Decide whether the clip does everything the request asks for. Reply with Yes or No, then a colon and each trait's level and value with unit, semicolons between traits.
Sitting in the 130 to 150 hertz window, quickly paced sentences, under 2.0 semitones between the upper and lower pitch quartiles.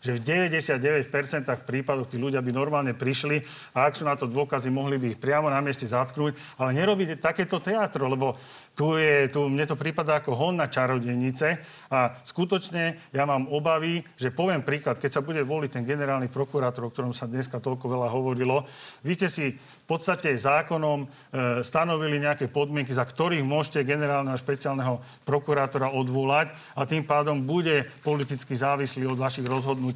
No: medium, 140 Hz; fast, 170 wpm; narrow, 2.6 semitones